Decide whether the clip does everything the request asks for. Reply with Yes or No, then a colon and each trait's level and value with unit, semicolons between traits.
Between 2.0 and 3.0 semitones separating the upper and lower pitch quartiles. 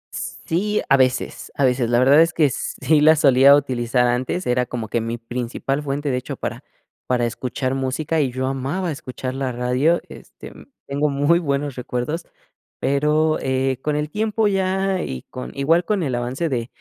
No: average, 3.8 semitones